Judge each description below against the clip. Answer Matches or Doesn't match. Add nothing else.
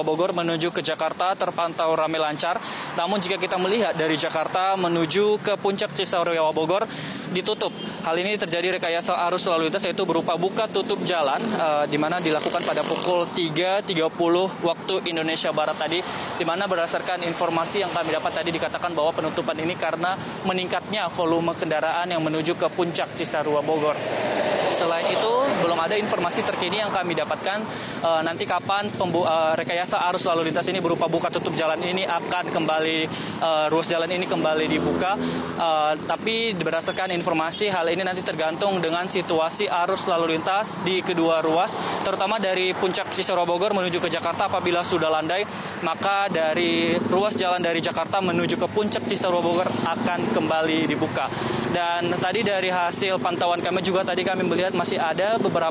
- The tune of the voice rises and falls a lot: Doesn't match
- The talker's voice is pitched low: Doesn't match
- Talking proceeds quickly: Matches